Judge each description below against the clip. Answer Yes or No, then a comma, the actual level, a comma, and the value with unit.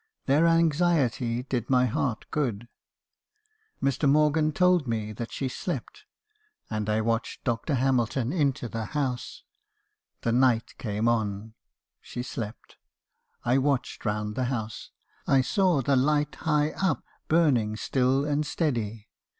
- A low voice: Yes, low, 130 Hz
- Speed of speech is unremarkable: No, slow, 130 wpm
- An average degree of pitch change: Yes, average, 4.4 semitones